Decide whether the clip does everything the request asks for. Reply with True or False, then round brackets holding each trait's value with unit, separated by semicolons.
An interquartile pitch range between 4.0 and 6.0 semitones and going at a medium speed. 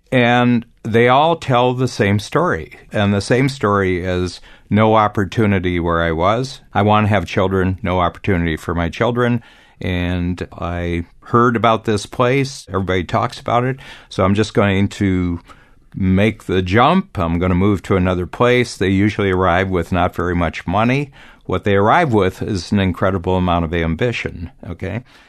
True (4.6 semitones; 170 wpm)